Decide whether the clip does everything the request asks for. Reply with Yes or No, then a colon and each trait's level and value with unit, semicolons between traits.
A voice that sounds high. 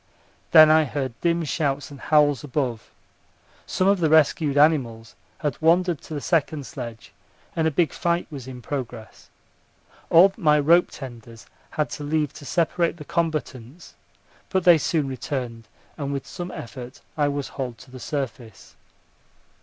No: medium, 145 Hz